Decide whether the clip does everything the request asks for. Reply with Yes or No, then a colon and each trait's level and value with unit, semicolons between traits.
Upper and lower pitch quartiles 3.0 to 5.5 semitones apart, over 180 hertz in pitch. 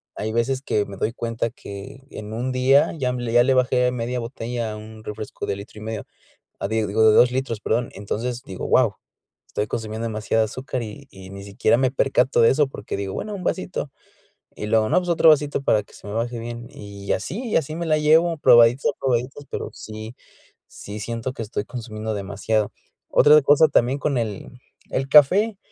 No: average, 3.8 semitones; low, 120 Hz